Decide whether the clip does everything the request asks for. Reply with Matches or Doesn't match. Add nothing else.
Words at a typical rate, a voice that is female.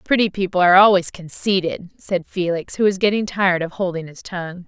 Matches